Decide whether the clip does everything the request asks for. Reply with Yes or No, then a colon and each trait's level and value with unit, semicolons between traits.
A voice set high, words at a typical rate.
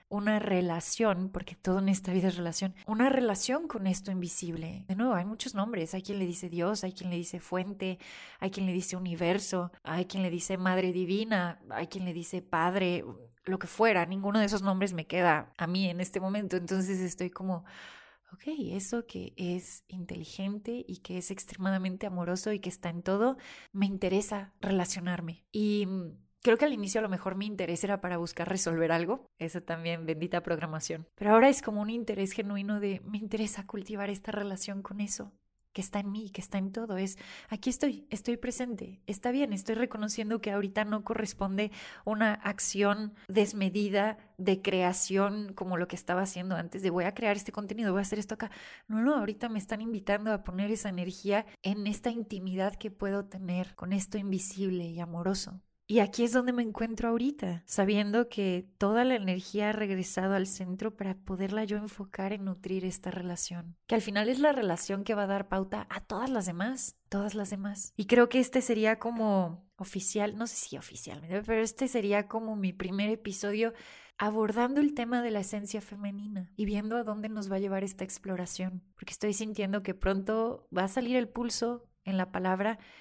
No: high, 200 Hz; fast, 195 wpm